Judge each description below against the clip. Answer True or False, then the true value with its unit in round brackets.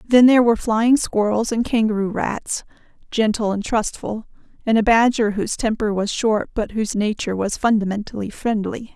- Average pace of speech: True (160 wpm)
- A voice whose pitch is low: False (220 Hz)